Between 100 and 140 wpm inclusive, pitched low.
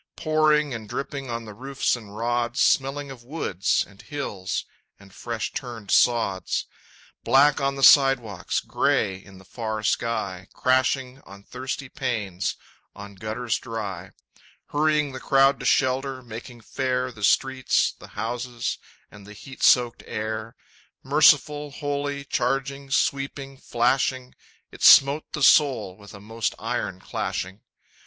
Yes: slow, 135 wpm; low, 125 Hz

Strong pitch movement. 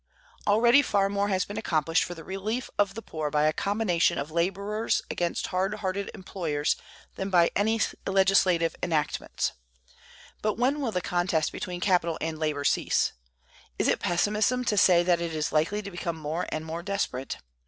No: average, 3.9 semitones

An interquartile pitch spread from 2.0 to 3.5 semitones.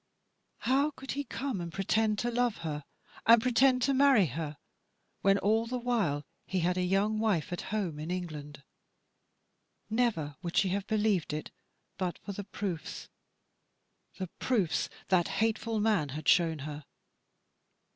No: wide, 5.6 semitones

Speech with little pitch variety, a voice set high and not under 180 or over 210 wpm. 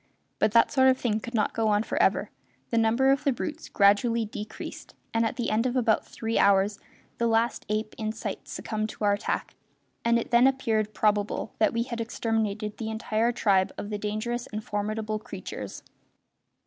Yes: narrow, 1.8 semitones; high, 220 Hz; average, 190 wpm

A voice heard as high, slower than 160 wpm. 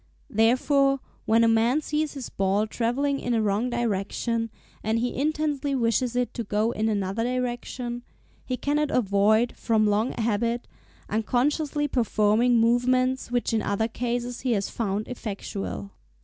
Yes: high, 235 Hz; average, 145 wpm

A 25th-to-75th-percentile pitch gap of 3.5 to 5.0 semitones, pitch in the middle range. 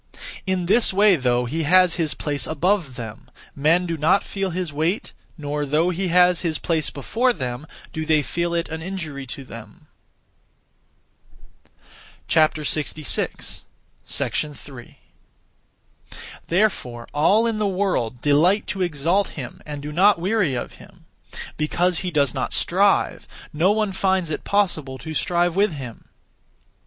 Yes: average, 4.3 semitones; medium, 165 Hz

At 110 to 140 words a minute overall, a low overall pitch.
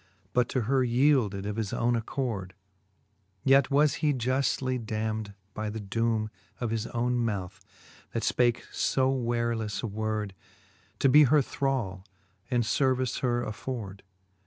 Yes: slow, 135 wpm; low, 120 Hz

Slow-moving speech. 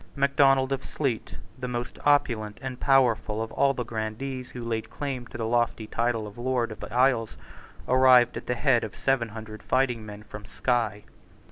No: average, 180 wpm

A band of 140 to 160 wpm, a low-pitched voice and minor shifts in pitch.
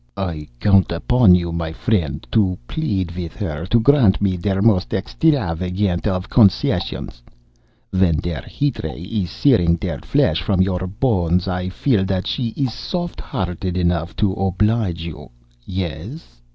No: average, 150 wpm; very low, 95 Hz; average, 3.6 semitones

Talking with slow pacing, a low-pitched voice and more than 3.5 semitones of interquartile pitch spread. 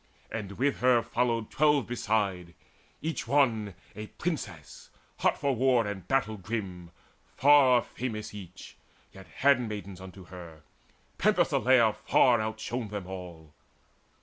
Yes: slow, 120 wpm; low, 110 Hz; average, 5.0 semitones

